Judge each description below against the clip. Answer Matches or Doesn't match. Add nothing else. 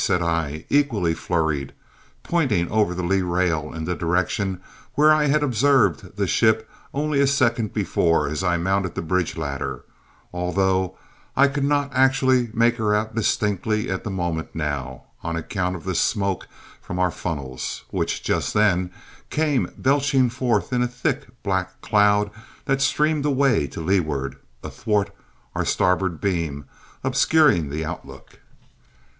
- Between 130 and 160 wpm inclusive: Matches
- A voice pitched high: Doesn't match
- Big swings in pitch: Matches